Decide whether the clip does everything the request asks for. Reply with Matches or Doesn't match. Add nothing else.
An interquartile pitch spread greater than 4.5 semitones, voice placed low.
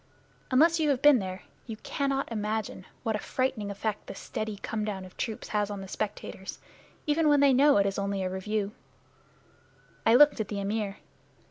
Doesn't match